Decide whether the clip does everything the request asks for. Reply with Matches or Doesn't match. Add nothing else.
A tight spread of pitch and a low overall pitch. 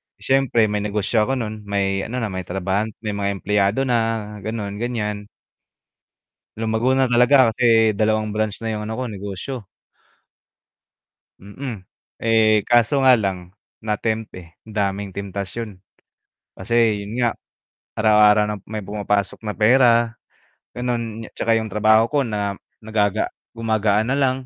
Matches